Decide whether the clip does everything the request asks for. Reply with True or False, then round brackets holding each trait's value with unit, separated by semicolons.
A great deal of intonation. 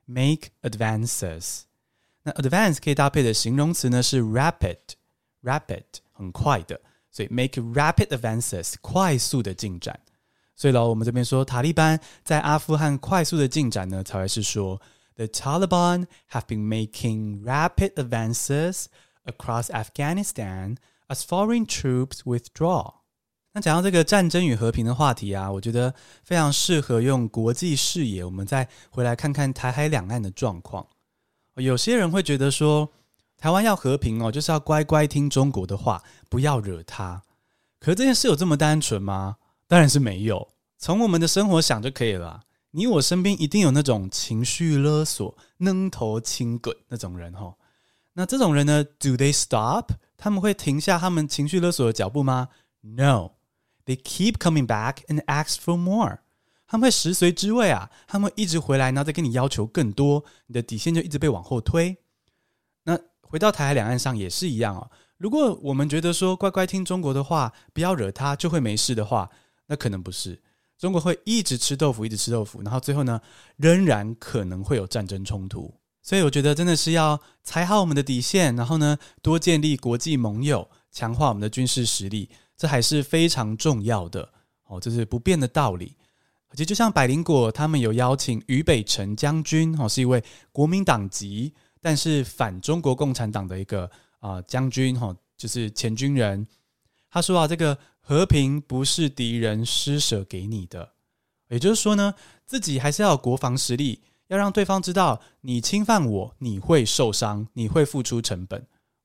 True (5.8 semitones)